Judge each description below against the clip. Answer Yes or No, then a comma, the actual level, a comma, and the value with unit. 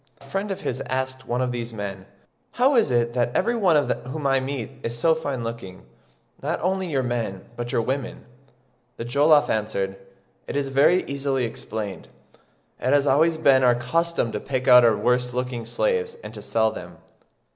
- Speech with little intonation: No, average, 3.6 semitones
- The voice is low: Yes, low, 130 Hz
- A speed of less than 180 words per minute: No, average, 185 wpm